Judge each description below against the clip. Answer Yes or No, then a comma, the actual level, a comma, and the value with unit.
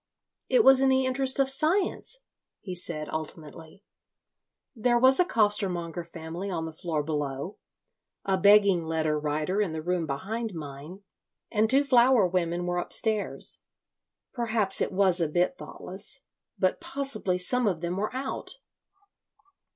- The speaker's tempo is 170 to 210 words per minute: No, average, 145 wpm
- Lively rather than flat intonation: Yes, wide, 6.5 semitones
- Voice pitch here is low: No, high, 190 Hz